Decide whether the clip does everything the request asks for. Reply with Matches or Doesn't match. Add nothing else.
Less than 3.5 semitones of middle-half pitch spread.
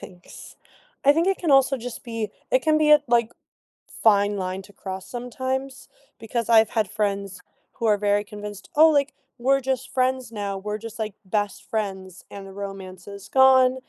Doesn't match